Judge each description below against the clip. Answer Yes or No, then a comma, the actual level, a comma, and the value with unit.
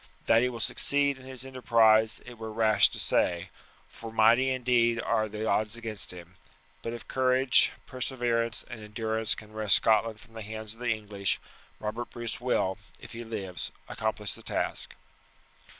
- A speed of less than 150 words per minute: No, average, 165 wpm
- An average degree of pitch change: No, narrow, 1.9 semitones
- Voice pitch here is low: Yes, low, 115 Hz